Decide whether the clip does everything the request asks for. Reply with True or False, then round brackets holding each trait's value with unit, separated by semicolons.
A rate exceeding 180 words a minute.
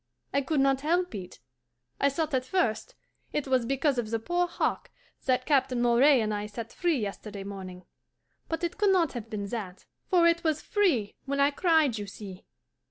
True (190 wpm)